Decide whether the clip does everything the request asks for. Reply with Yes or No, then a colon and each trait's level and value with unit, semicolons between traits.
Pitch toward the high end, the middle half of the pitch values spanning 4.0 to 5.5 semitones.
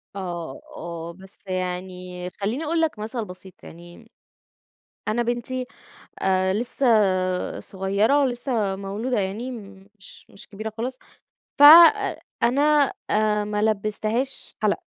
Yes: high, 210 Hz; average, 4.5 semitones